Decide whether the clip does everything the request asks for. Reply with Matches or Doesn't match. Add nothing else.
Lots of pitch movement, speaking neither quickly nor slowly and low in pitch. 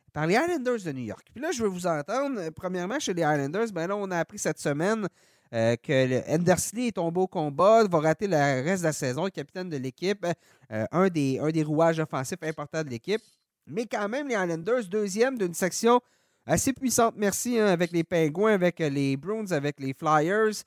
Doesn't match